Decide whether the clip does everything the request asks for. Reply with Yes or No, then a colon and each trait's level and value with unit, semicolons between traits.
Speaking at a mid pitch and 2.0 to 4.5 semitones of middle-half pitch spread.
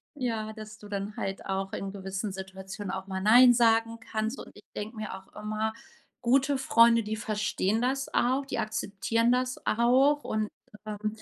No: high, 215 Hz; average, 2.8 semitones